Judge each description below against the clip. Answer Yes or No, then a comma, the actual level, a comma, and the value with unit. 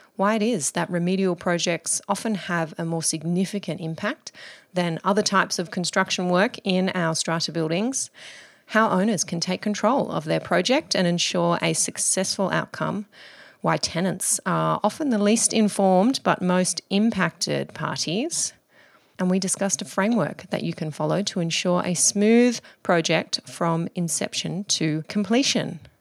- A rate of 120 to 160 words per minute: Yes, average, 150 wpm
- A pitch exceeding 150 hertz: Yes, medium, 185 Hz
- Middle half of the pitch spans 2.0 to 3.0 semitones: No, average, 3.6 semitones